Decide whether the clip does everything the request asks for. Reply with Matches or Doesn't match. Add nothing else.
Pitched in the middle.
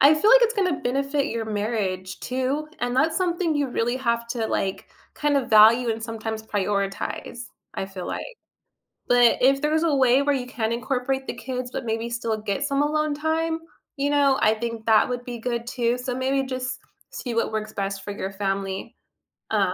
Doesn't match